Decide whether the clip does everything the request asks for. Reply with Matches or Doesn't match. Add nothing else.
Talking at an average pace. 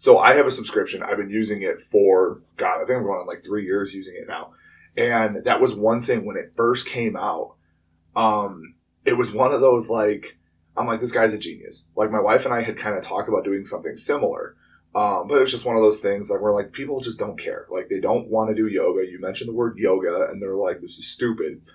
Doesn't match